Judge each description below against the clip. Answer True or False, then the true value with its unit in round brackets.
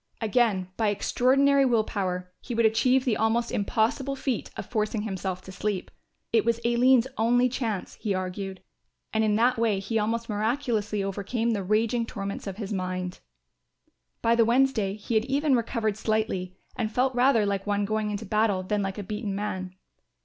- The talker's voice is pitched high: True (220 Hz)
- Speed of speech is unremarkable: True (175 wpm)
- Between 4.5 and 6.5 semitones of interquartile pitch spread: False (3.0 semitones)